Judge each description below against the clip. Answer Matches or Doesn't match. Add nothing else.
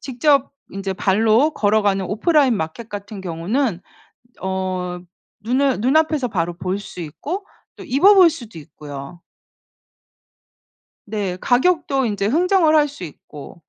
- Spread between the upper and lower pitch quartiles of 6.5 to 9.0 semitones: Matches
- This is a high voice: Matches